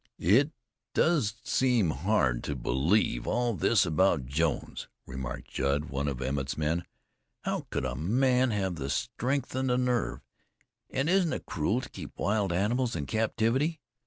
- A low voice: Yes, low, 100 Hz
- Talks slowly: No, average, 155 wpm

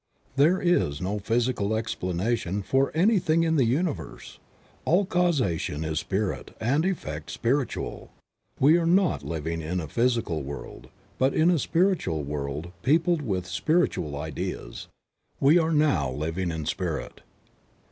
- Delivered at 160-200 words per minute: No, slow, 135 wpm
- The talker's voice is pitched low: Yes, low, 115 Hz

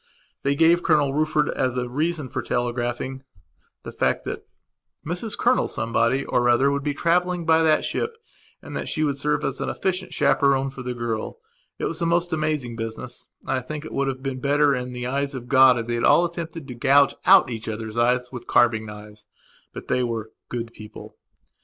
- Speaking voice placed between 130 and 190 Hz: Yes, low, 135 Hz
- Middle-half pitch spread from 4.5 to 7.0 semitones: No, average, 4.0 semitones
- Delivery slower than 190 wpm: No, fast, 205 wpm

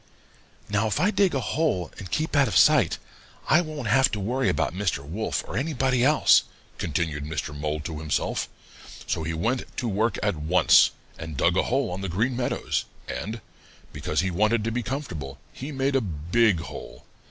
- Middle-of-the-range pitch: No, low, 105 Hz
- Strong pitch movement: Yes, wide, 8.2 semitones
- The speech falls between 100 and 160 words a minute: No, average, 185 wpm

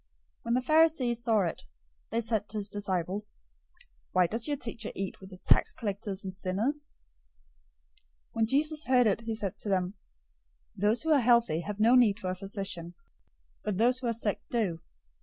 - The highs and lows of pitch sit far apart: No, average, 3.7 semitones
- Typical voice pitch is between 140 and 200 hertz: No, high, 215 Hz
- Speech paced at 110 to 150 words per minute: No, average, 180 wpm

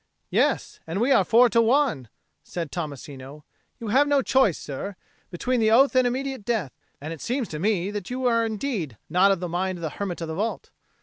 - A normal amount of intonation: No, wide, 6.6 semitones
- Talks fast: Yes, fast, 210 wpm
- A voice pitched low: No, high, 205 Hz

